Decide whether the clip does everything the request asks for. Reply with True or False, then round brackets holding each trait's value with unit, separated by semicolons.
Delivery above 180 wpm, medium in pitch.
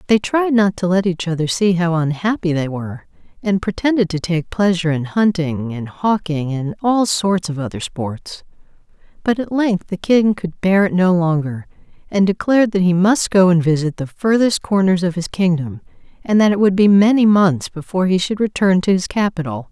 True (200 wpm; 180 Hz)